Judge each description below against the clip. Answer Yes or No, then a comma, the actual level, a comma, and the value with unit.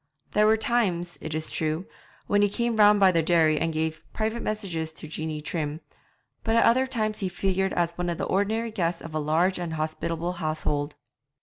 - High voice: No, medium, 175 Hz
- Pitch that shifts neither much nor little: Yes, average, 4.8 semitones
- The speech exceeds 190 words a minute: Yes, average, 200 wpm